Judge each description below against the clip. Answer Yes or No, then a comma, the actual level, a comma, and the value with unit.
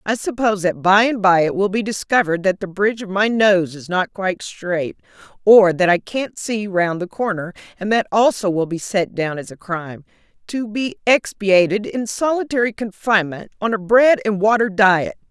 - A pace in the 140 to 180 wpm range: No, average, 195 wpm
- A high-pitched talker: Yes, high, 200 Hz